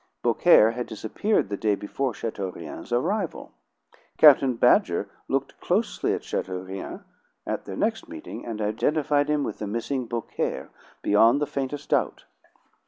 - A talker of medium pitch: No, low, 120 Hz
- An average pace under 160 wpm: Yes, slow, 135 wpm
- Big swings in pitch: Yes, wide, 5.8 semitones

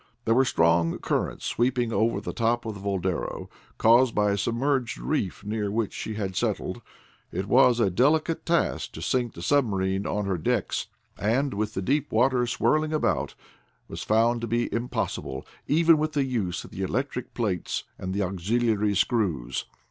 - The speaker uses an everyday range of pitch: Yes, average, 4.4 semitones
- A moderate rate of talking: Yes, average, 170 wpm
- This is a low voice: Yes, low, 115 Hz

